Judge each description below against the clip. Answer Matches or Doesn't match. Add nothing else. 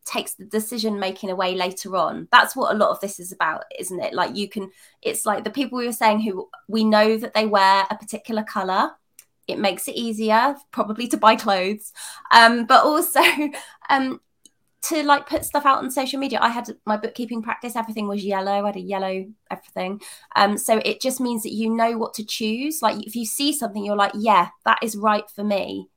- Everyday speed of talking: Doesn't match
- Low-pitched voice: Doesn't match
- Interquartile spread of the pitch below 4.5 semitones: Matches